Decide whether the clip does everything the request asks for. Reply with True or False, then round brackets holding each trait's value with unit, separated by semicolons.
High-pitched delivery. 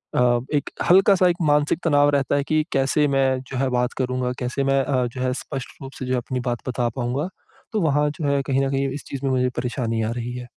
False (135 Hz)